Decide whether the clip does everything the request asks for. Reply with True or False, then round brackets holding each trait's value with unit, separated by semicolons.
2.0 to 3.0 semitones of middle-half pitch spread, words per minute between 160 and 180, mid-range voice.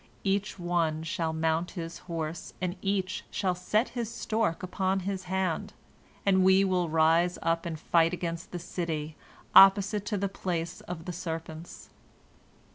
False (2.5 semitones; 150 wpm; 175 Hz)